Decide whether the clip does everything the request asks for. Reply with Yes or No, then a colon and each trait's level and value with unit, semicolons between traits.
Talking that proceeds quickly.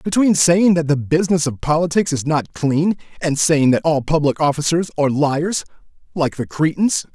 No: average, 175 wpm